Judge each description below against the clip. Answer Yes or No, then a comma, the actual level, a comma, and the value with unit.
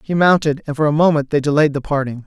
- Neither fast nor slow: No, fast, 265 wpm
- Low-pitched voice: No, medium, 150 Hz